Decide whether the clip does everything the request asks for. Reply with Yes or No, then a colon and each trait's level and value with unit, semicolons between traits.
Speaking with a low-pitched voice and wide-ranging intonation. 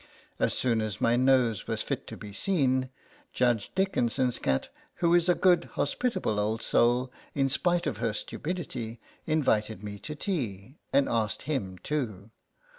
Yes: low, 125 Hz; wide, 5.8 semitones